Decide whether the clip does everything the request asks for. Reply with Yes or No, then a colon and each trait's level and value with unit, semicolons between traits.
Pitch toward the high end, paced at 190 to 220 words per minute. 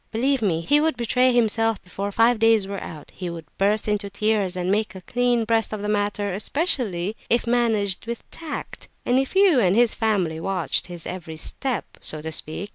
Yes: high, 210 Hz; average, 200 wpm